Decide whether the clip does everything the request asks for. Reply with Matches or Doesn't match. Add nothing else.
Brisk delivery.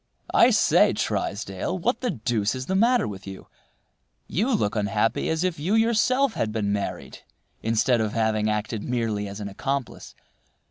Doesn't match